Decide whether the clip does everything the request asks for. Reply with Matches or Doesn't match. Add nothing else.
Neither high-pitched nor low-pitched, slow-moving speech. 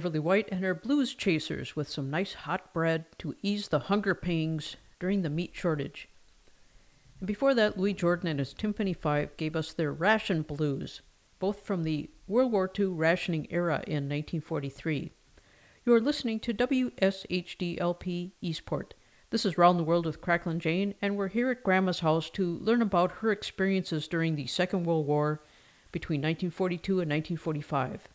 Doesn't match